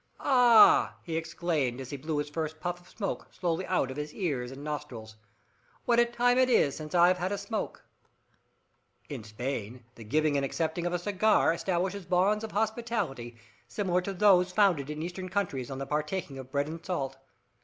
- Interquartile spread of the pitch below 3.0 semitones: No, wide, 5.4 semitones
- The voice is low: No, medium, 165 Hz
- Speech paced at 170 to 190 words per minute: Yes, average, 185 wpm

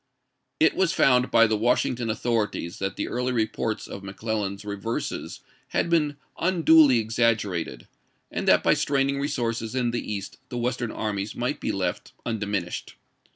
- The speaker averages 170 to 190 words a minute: No, average, 155 wpm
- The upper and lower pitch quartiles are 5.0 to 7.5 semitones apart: No, average, 3.4 semitones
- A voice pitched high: No, low, 115 Hz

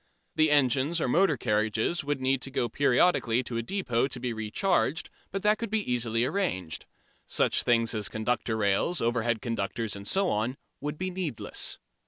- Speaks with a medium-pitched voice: No, low, 125 Hz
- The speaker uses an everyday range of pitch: No, wide, 5.8 semitones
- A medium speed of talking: Yes, average, 180 wpm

